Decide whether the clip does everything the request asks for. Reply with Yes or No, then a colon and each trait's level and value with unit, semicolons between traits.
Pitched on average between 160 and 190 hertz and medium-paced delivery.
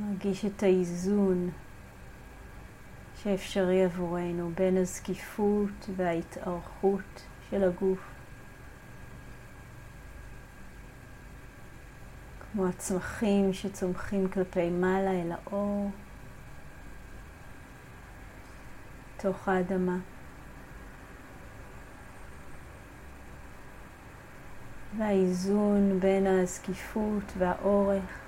No: medium, 185 Hz; slow, 50 wpm